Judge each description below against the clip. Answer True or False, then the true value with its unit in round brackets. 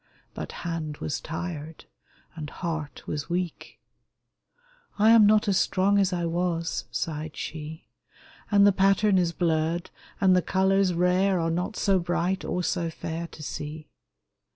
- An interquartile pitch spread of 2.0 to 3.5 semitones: True (3.0 semitones)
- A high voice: False (175 Hz)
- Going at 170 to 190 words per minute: False (155 wpm)